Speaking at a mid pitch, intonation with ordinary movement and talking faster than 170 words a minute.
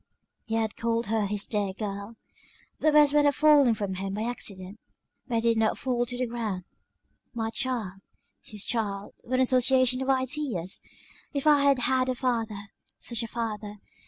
No: high, 230 Hz; average, 3.7 semitones; average, 180 wpm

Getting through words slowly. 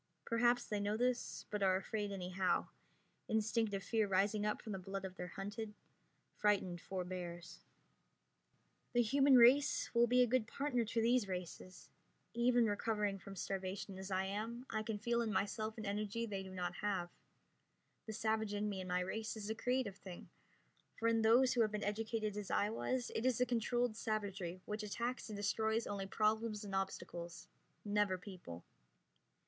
No: average, 175 wpm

